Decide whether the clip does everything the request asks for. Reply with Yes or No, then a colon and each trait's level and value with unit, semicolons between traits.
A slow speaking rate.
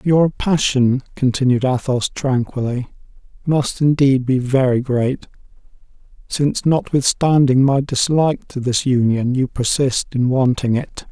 Yes: slow, 120 wpm